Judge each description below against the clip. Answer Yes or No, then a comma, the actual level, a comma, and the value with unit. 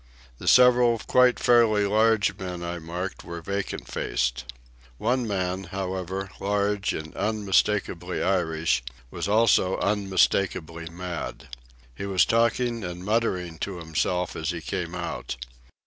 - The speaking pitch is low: Yes, very low, 95 Hz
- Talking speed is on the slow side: Yes, slow, 125 wpm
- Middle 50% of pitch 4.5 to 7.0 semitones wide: No, average, 3.4 semitones